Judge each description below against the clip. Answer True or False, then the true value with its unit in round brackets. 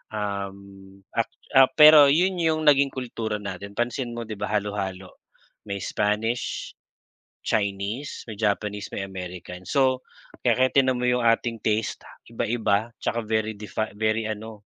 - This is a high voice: False (110 Hz)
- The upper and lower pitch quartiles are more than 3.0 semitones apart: True (3.4 semitones)